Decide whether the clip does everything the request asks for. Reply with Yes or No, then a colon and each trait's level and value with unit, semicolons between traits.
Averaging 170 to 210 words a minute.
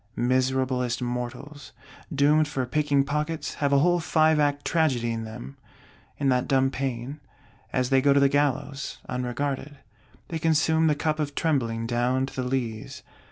No: average, 160 wpm